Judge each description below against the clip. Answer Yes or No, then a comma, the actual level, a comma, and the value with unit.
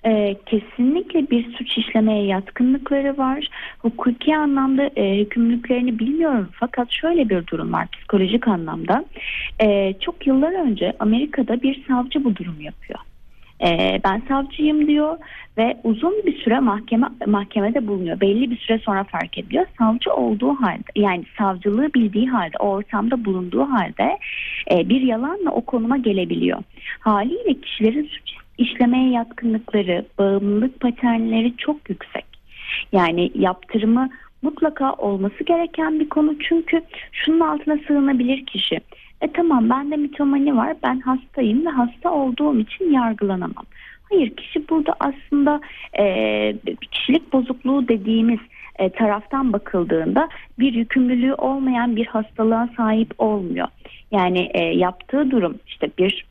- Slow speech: No, average, 125 wpm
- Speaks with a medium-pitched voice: No, high, 245 Hz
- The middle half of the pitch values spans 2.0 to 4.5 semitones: No, average, 5.0 semitones